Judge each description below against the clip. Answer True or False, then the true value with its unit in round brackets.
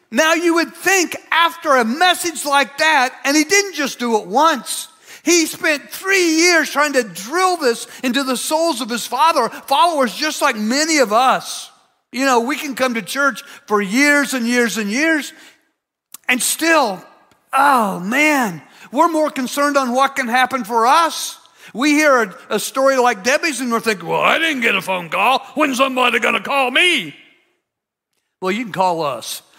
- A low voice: False (275 Hz)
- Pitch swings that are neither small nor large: True (4.5 semitones)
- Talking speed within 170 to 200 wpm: True (180 wpm)